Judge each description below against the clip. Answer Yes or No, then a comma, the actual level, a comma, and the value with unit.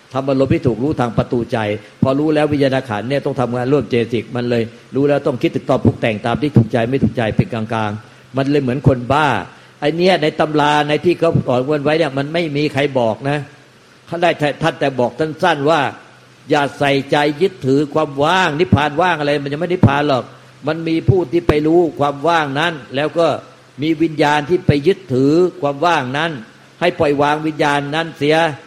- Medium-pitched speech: Yes, medium, 145 Hz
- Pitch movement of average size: Yes, average, 3.8 semitones